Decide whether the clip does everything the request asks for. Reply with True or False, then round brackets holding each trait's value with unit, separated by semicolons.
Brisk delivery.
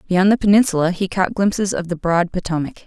True (210 wpm)